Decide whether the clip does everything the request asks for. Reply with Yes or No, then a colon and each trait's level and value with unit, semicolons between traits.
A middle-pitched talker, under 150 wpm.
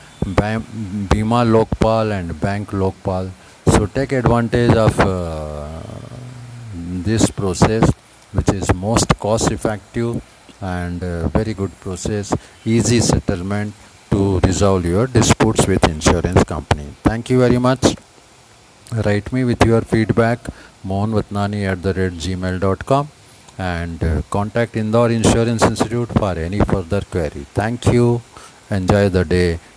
No: low, 105 Hz; average, 120 wpm